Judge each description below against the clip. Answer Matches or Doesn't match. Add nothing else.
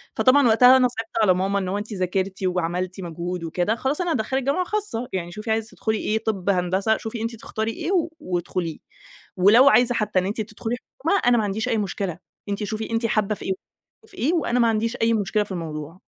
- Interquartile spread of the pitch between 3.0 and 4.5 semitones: Matches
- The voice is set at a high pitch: Matches